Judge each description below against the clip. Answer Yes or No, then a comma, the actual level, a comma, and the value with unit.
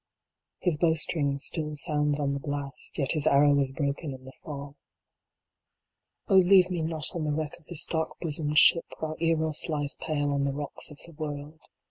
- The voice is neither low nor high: Yes, medium, 150 Hz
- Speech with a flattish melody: Yes, narrow, 2.0 semitones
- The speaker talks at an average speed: Yes, average, 185 wpm